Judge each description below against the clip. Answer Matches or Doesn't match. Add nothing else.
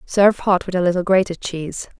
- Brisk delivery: Matches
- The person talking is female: Matches